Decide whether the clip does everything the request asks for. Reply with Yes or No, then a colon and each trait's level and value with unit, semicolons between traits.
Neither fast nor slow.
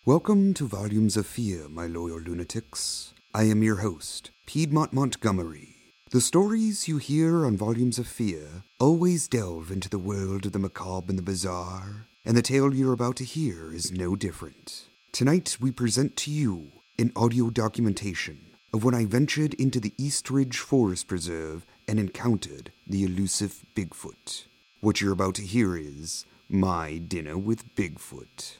Yes: average, 160 wpm